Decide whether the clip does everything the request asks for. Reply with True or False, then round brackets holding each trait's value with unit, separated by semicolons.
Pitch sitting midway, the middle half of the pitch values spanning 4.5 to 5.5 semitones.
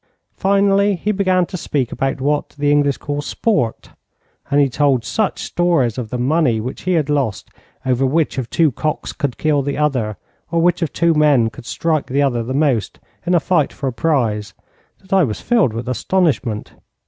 True (145 Hz; 5.0 semitones)